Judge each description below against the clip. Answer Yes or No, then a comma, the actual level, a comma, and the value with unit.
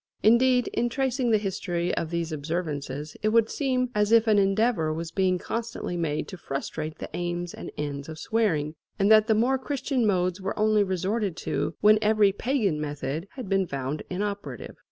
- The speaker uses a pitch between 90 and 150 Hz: No, high, 195 Hz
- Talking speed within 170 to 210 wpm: Yes, average, 180 wpm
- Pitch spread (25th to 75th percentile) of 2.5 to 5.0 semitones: No, wide, 5.4 semitones